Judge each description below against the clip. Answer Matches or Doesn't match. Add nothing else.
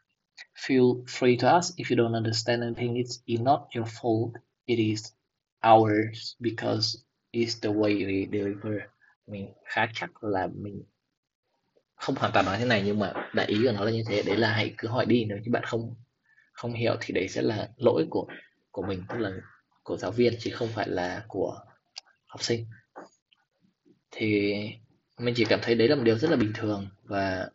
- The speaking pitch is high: Doesn't match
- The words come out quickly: Doesn't match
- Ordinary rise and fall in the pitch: Doesn't match